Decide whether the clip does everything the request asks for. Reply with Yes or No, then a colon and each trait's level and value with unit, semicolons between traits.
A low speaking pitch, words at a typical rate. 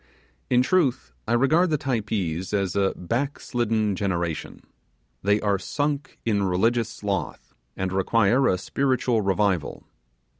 No: low, 105 Hz; slow, 125 wpm